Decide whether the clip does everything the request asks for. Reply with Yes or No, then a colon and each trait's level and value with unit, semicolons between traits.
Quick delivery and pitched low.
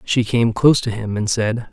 Yes: fast, 245 wpm; low, 110 Hz